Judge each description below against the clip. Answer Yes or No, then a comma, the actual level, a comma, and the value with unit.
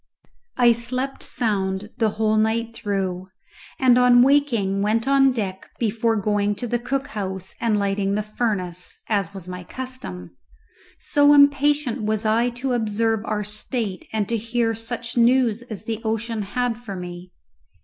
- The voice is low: No, high, 225 Hz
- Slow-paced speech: No, average, 155 wpm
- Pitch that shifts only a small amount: No, average, 3.2 semitones